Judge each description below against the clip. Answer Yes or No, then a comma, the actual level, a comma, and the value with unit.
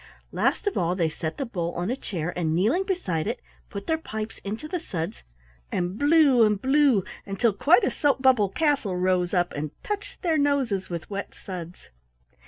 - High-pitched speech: Yes, high, 205 Hz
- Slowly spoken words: No, average, 190 wpm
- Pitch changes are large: Yes, wide, 8.1 semitones